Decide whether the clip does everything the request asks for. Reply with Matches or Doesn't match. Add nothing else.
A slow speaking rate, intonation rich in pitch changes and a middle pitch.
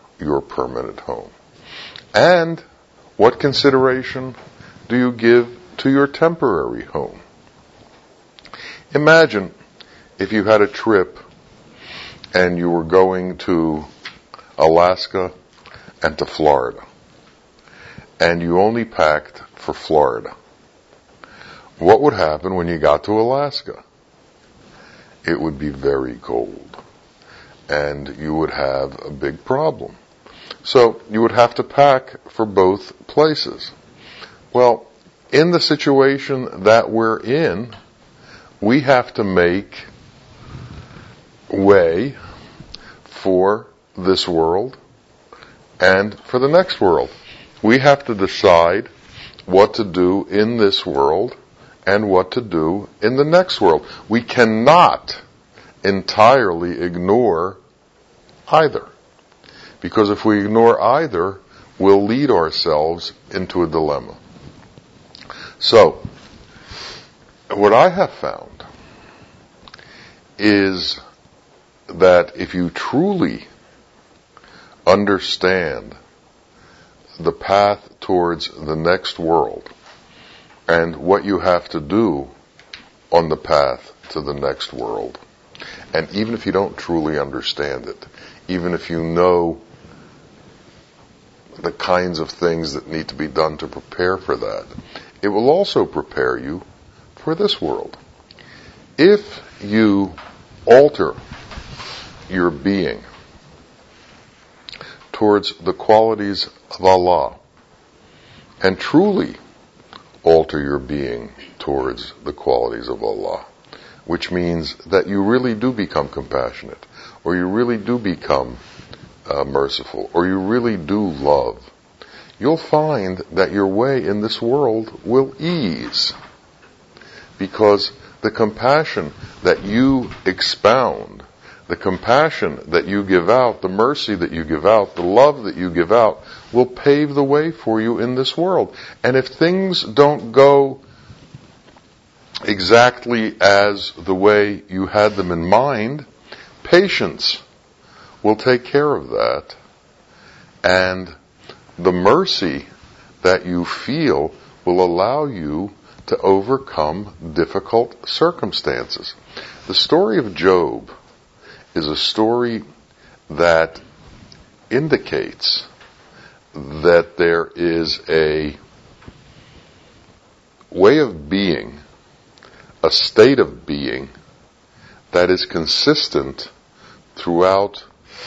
Doesn't match